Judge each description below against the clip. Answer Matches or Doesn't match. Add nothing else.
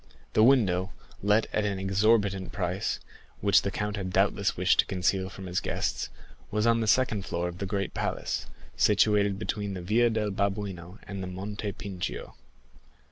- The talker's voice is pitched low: Matches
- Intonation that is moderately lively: Doesn't match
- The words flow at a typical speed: Matches